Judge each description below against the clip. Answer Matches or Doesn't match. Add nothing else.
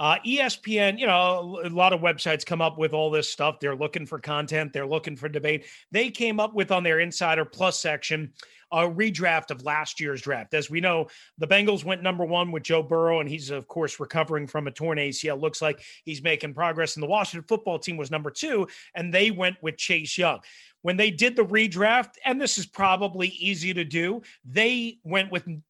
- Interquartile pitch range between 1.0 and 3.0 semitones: Doesn't match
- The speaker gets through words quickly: Matches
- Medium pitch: Matches